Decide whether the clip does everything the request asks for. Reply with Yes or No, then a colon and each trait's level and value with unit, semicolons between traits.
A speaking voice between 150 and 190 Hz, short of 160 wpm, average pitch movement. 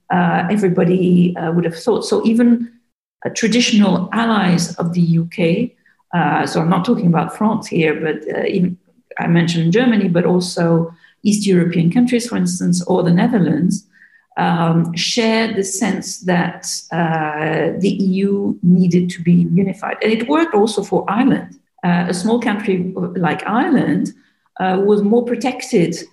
Yes: medium, 185 Hz; average, 150 wpm; average, 4.0 semitones